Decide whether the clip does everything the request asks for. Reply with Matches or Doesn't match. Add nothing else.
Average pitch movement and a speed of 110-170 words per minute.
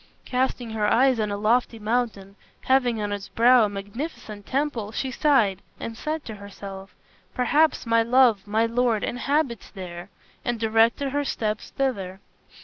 Matches